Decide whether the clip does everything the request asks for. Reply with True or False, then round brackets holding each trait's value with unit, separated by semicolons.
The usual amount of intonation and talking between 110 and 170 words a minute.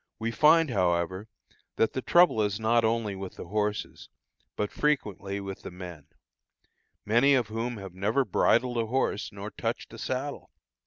True (3.8 semitones; 160 wpm)